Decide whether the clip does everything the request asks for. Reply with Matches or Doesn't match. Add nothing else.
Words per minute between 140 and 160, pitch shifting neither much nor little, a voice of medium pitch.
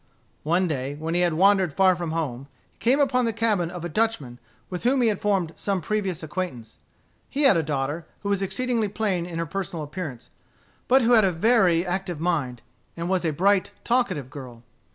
Doesn't match